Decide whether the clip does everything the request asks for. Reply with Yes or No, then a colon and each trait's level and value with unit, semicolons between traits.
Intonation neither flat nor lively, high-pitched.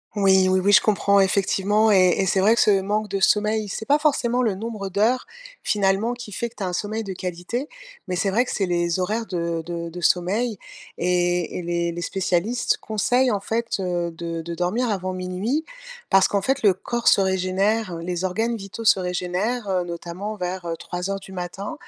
Yes: average, 3.4 semitones; high, 195 Hz